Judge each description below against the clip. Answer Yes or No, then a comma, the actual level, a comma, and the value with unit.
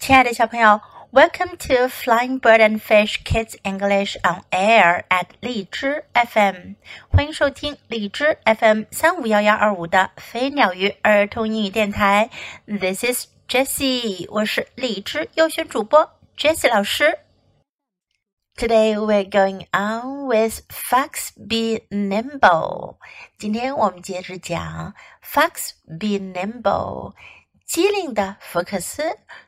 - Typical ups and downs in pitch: Yes, average, 4.5 semitones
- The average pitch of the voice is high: Yes, high, 220 Hz